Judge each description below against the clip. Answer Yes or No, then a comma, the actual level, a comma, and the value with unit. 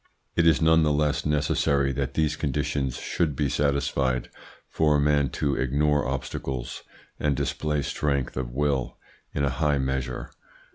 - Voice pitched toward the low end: Yes, very low, 70 Hz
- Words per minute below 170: Yes, average, 150 wpm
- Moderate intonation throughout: No, narrow, 2.0 semitones